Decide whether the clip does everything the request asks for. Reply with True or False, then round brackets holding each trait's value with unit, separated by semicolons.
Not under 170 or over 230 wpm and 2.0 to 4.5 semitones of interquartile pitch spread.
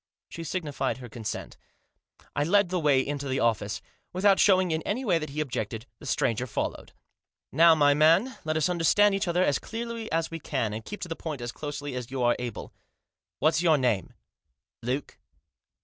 False (195 wpm; 5.5 semitones)